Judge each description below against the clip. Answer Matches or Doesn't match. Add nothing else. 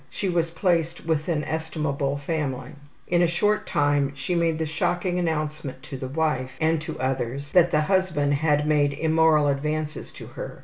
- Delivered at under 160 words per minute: Doesn't match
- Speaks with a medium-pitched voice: Matches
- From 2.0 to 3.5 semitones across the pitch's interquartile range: Matches